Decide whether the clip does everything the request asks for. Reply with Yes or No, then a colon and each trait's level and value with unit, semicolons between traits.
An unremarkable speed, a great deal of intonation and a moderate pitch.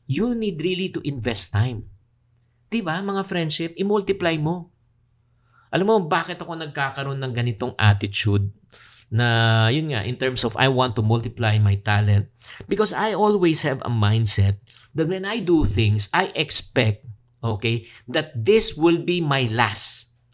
No: average, 150 wpm; wide, 6.7 semitones; low, 125 Hz